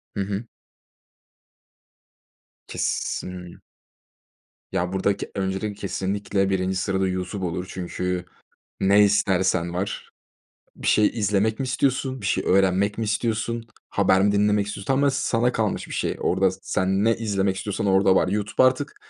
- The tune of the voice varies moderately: No, narrow, 2.2 semitones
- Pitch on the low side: Yes, low, 100 Hz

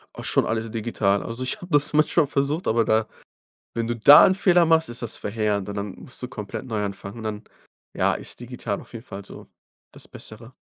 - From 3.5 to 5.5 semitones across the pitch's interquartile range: Yes, average, 4.6 semitones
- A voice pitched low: Yes, low, 115 Hz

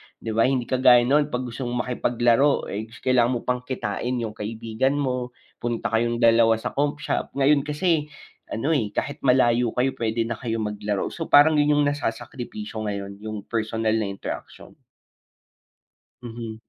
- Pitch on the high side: No, low, 120 Hz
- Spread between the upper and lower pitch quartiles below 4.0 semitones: Yes, average, 3.0 semitones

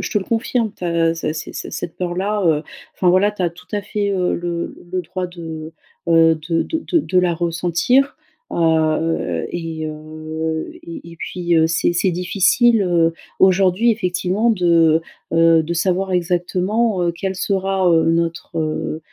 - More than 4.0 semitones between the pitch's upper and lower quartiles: No, average, 2.7 semitones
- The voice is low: No, medium, 175 Hz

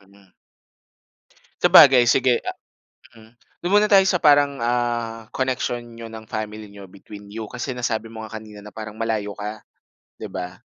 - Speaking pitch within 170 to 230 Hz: No, low, 110 Hz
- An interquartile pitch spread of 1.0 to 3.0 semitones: Yes, average, 2.7 semitones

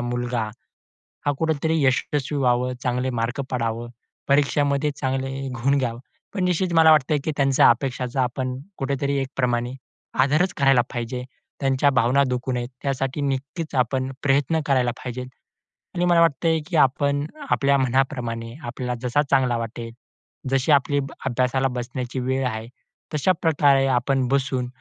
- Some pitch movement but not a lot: No, narrow, 2.3 semitones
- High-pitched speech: No, low, 135 Hz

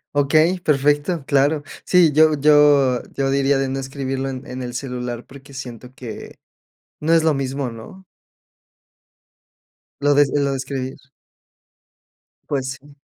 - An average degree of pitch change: No, narrow, 1.9 semitones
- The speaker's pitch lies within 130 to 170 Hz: Yes, medium, 140 Hz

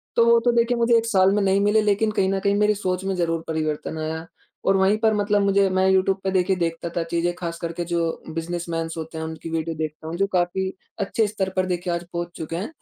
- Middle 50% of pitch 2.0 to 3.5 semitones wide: Yes, average, 3.2 semitones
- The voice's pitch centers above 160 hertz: Yes, medium, 185 Hz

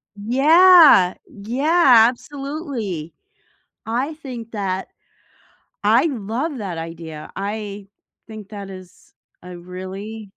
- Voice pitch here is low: No, high, 215 Hz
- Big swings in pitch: Yes, wide, 6.1 semitones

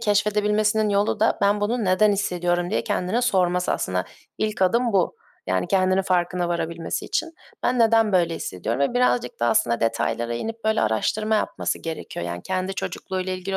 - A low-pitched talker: No, high, 190 Hz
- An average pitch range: Yes, average, 3.9 semitones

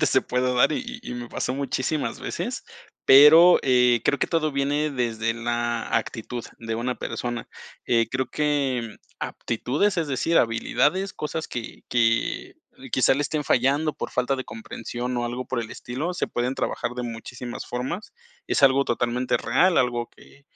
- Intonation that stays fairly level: No, average, 3.4 semitones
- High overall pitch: No, low, 125 Hz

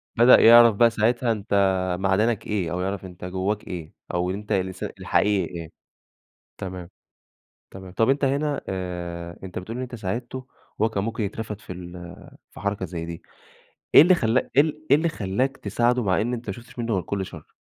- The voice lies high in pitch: No, low, 100 Hz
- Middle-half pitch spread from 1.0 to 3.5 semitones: No, average, 4.4 semitones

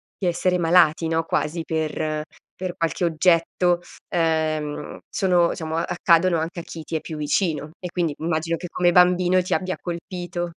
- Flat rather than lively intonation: Yes, narrow, 1.9 semitones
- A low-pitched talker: No, medium, 170 Hz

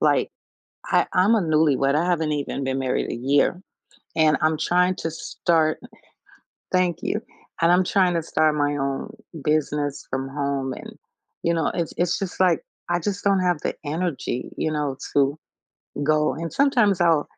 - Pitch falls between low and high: Yes, medium, 155 Hz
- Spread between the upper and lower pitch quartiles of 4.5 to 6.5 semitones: No, average, 3.6 semitones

